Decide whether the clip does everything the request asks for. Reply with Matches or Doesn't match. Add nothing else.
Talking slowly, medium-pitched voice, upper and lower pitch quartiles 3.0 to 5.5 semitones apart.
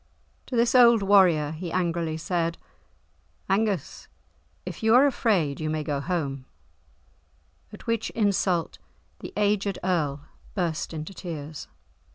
Matches